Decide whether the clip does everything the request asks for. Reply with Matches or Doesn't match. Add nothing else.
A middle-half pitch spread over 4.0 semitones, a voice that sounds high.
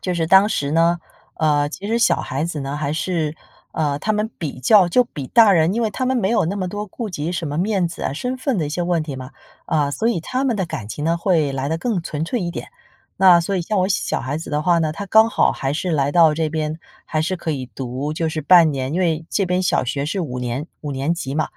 Doesn't match